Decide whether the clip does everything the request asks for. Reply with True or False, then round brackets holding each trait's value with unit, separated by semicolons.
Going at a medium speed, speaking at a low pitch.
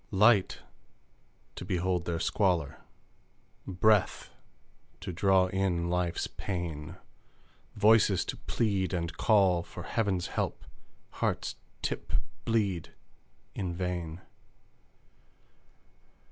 False (90 wpm; 90 Hz)